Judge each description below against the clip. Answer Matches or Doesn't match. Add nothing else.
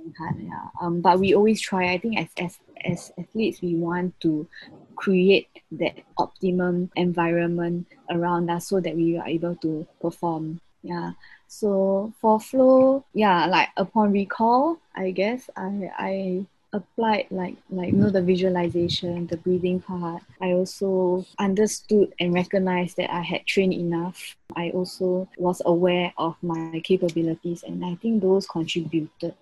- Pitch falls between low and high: Matches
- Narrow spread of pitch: Matches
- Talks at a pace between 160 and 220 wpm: Doesn't match